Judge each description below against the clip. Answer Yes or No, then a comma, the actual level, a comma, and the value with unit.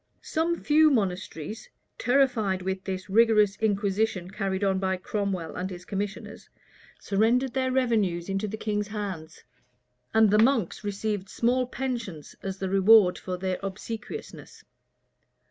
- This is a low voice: No, high, 205 Hz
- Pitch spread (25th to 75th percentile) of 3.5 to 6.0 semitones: No, average, 3.1 semitones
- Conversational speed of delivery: No, slow, 130 wpm